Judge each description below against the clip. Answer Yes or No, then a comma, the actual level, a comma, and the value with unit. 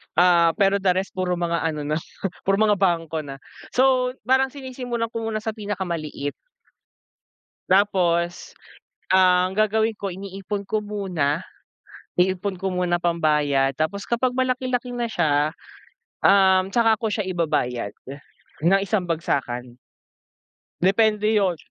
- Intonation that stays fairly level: No, average, 4.2 semitones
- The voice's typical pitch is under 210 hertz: Yes, high, 190 Hz